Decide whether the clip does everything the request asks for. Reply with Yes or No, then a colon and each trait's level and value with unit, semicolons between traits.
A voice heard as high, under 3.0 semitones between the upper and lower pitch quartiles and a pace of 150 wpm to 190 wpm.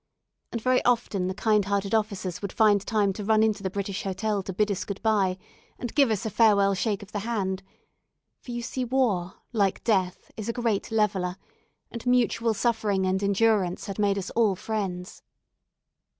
Yes: high, 205 Hz; narrow, 2.6 semitones; average, 185 wpm